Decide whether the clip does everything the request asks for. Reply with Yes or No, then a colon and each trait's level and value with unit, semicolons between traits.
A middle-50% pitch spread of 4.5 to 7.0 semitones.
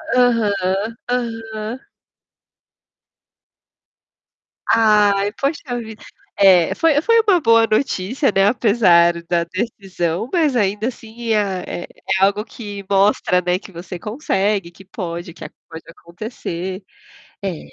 No: average, 3.9 semitones